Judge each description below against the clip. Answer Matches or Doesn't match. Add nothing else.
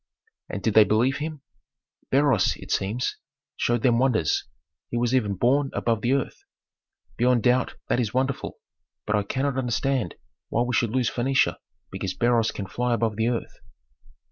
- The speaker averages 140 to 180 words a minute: Matches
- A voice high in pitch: Doesn't match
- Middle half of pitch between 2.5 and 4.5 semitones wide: Matches